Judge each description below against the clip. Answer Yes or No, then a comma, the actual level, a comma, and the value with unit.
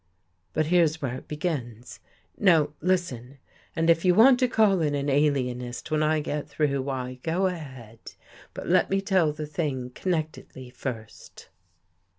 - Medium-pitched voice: Yes, medium, 150 Hz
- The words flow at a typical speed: Yes, average, 155 wpm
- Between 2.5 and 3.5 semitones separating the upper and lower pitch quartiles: No, average, 4.7 semitones